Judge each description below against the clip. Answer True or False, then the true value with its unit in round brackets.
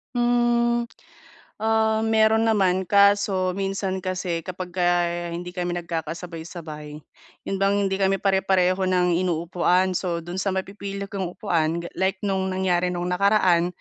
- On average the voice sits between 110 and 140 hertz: False (185 Hz)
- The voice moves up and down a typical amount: False (2.1 semitones)